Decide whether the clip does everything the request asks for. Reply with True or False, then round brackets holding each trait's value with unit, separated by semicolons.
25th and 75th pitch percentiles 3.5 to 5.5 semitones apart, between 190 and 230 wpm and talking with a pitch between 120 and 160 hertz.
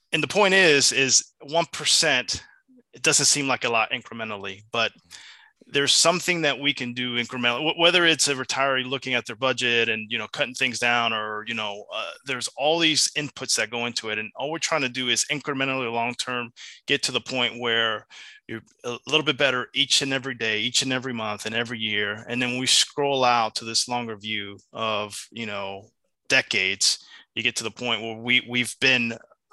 True (3.8 semitones; 205 wpm; 125 Hz)